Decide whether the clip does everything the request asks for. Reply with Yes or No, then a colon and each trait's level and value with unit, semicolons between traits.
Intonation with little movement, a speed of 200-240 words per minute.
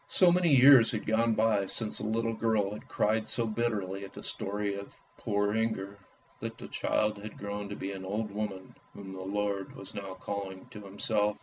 Yes: narrow, 2.0 semitones; fast, 205 wpm